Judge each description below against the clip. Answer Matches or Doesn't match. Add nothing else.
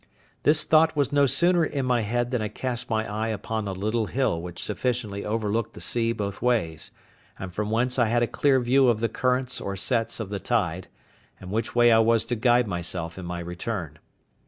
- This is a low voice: Matches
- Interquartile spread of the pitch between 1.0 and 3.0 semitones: Doesn't match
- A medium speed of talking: Doesn't match